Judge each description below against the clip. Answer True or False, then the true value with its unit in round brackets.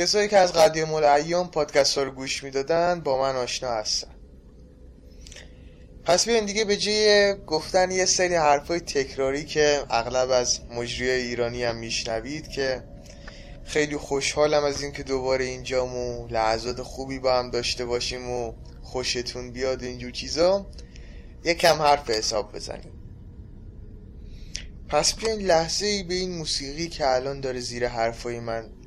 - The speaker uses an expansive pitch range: False (5.0 semitones)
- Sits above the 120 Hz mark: True (130 Hz)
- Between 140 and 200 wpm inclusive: True (145 wpm)